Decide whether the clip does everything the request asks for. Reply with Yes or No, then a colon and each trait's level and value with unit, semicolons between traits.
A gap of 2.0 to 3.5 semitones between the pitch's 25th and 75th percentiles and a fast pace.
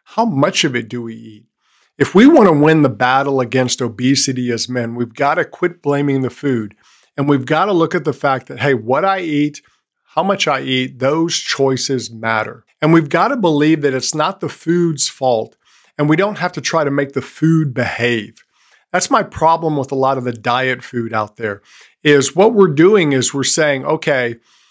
No: average, 4.2 semitones; fast, 210 wpm